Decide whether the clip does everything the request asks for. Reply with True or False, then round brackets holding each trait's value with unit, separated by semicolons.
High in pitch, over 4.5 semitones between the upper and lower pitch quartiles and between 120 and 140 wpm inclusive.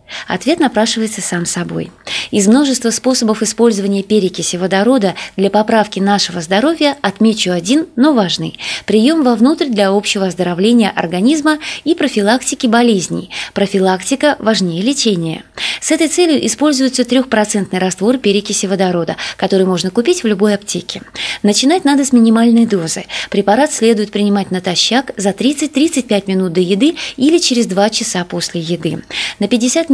True (215 Hz; 5.2 semitones; 130 wpm)